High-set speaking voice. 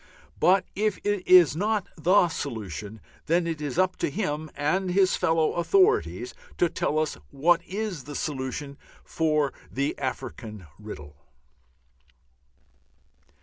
No: medium, 160 Hz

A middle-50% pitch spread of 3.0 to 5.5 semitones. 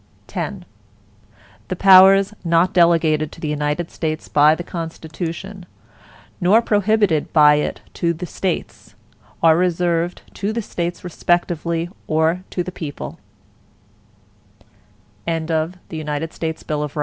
No: narrow, 2.5 semitones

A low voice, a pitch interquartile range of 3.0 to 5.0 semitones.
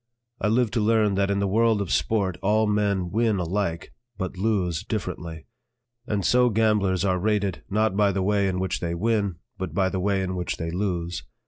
No: low, 100 Hz; narrow, 2.5 semitones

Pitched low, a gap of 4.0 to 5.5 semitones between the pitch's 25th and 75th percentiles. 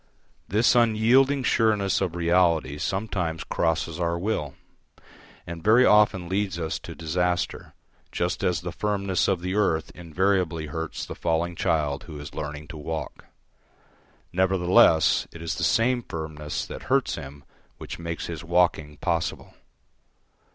No: very low, 85 Hz; average, 3.3 semitones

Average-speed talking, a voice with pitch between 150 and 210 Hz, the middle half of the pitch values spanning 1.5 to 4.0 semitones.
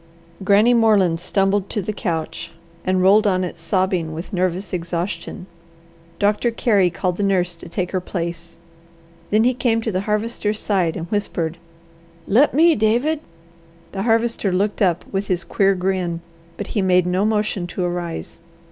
Yes: average, 160 wpm; high, 190 Hz; average, 3.1 semitones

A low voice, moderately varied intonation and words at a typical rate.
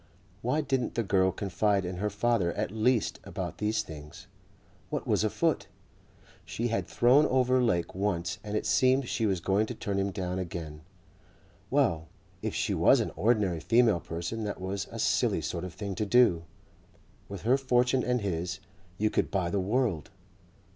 Yes: low, 100 Hz; average, 4.8 semitones; average, 175 wpm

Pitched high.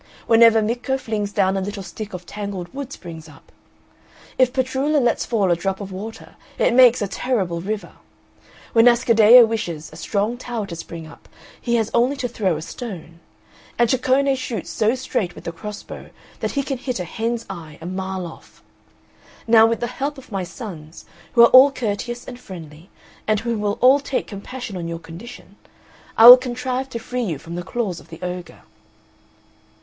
Yes: high, 220 Hz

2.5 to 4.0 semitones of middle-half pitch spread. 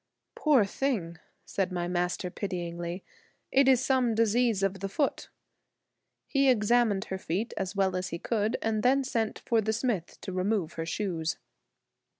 No: average, 4.6 semitones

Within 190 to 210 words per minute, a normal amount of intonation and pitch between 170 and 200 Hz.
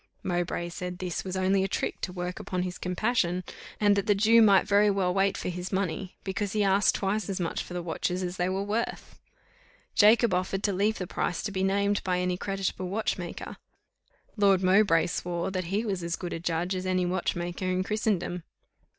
No: average, 200 wpm; narrow, 2.0 semitones; medium, 185 Hz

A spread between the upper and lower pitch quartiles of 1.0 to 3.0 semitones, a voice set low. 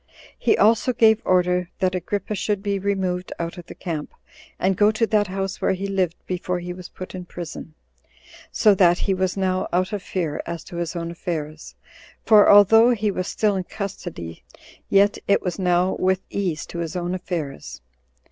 No: narrow, 2.4 semitones; medium, 185 Hz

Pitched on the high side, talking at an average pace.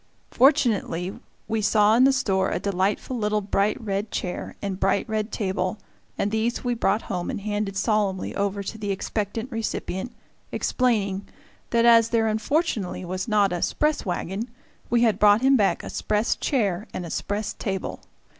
Yes: high, 210 Hz; average, 165 wpm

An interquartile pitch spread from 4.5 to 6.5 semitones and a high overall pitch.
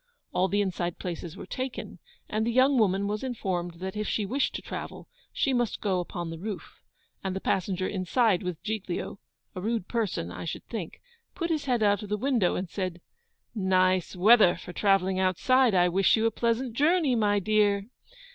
No: average, 3.9 semitones; high, 200 Hz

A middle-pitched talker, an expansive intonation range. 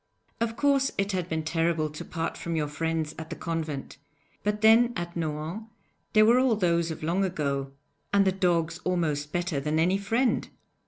No: medium, 170 Hz; average, 4.1 semitones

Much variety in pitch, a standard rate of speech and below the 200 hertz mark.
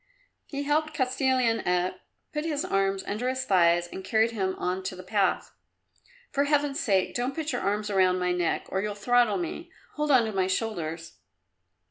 No: wide, 5.9 semitones; average, 180 wpm; high, 210 Hz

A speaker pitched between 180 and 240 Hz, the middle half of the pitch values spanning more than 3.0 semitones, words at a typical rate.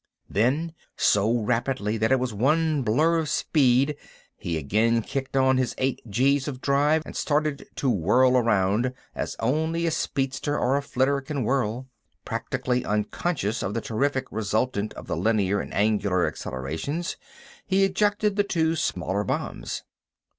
No: low, 130 Hz; average, 5.2 semitones; average, 150 wpm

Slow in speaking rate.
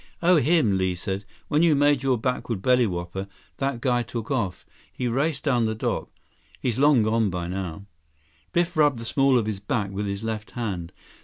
No: average, 185 wpm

